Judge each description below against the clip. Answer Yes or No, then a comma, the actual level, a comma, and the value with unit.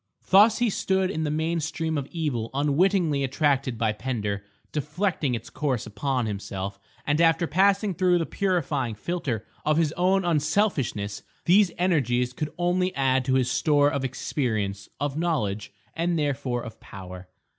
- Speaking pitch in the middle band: Yes, medium, 145 Hz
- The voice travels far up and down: Yes, wide, 5.9 semitones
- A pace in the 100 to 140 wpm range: No, average, 155 wpm